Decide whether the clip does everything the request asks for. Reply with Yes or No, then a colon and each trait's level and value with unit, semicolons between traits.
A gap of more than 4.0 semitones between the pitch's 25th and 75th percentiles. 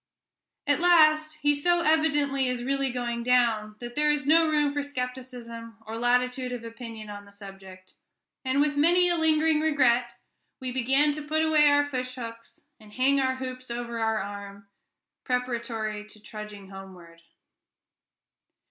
Yes: average, 4.4 semitones